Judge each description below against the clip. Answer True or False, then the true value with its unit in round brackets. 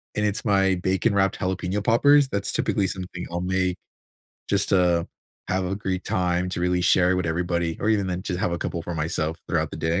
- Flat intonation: True (1.8 semitones)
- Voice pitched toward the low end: True (90 Hz)